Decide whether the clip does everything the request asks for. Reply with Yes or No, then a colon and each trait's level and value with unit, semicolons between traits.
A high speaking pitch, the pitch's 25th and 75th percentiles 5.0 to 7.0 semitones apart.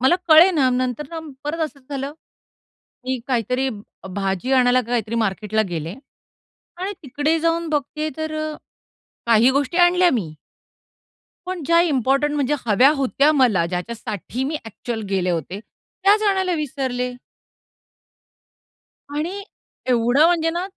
Yes: very high, 265 Hz; average, 5.3 semitones